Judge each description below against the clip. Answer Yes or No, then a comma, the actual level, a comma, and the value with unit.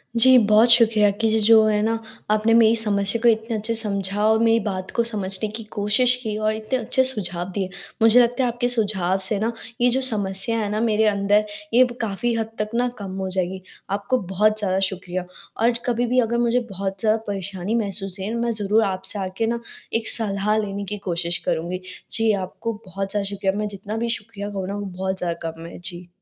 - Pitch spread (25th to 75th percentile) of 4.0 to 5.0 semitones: No, average, 2.9 semitones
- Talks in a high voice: Yes, high, 210 Hz